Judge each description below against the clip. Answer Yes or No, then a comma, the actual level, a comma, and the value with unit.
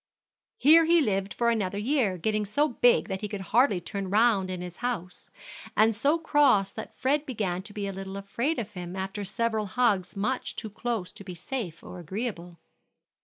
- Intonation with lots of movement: No, average, 4.1 semitones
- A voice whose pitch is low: No, high, 210 Hz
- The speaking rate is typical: Yes, average, 190 wpm